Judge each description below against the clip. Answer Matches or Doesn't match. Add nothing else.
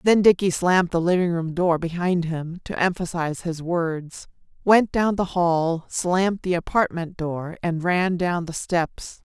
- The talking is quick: Doesn't match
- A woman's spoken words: Matches